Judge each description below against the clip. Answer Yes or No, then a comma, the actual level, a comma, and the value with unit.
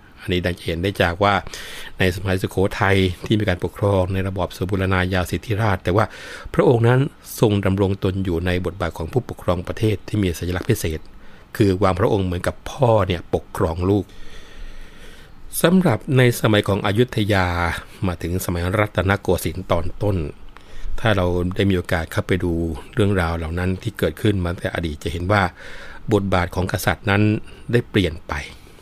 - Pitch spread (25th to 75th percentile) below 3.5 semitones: Yes, average, 2.8 semitones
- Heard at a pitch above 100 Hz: No, very low, 95 Hz